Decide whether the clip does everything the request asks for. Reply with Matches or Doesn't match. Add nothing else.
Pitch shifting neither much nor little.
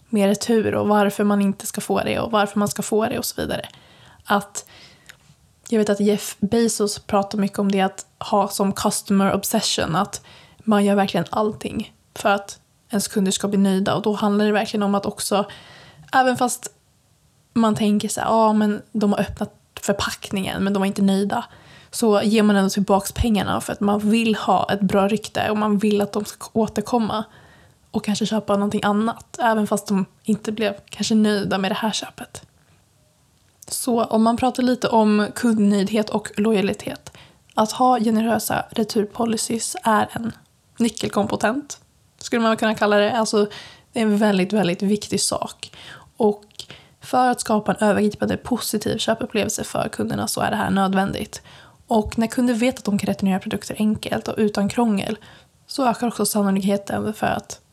Doesn't match